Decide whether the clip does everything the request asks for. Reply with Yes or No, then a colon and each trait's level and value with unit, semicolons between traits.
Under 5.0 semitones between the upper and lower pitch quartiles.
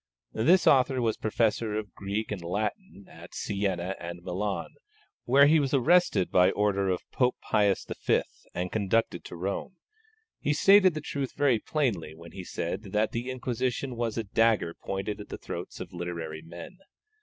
No: wide, 5.6 semitones